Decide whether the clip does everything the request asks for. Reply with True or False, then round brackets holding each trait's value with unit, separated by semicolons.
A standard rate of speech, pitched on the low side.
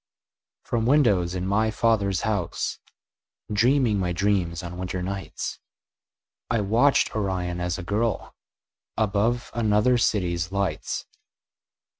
False (110 wpm; 100 Hz)